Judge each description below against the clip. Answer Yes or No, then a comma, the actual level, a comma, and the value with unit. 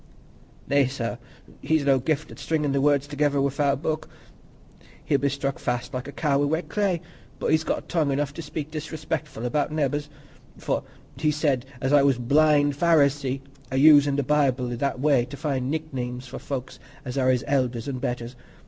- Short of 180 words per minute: No, average, 190 wpm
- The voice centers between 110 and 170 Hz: Yes, medium, 140 Hz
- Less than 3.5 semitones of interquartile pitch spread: Yes, narrow, 2.4 semitones